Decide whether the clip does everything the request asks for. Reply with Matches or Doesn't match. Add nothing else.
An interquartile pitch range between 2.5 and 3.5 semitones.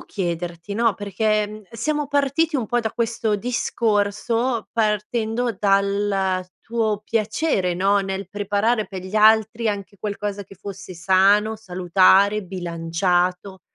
Matches